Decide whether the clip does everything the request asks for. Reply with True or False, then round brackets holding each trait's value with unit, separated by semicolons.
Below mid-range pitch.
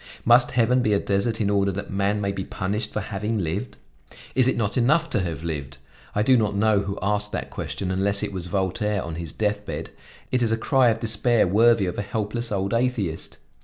True (105 Hz)